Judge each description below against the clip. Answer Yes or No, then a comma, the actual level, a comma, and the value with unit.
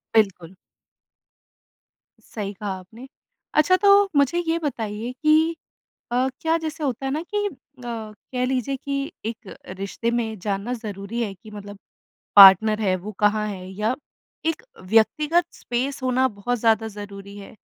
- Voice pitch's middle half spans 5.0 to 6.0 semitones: Yes, average, 5.3 semitones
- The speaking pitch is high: Yes, high, 225 Hz